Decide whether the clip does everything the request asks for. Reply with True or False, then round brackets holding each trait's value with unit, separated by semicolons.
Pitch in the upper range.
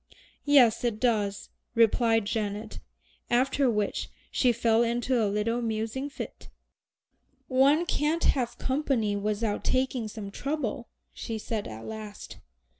True (230 Hz)